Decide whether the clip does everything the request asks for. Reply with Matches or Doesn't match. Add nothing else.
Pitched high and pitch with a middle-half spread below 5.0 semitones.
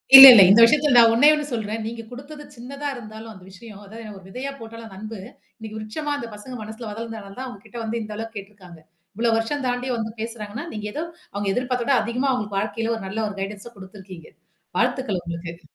Matches